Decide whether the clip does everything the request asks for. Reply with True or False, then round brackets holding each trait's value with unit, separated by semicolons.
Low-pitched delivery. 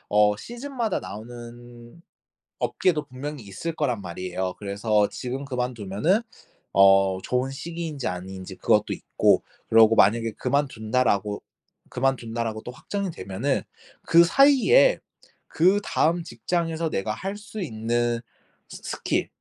True (120 Hz)